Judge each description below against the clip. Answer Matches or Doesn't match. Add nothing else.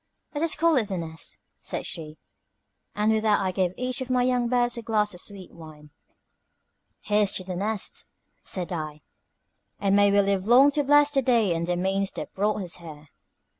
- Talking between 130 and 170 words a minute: Doesn't match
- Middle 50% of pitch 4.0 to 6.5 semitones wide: Matches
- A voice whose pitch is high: Matches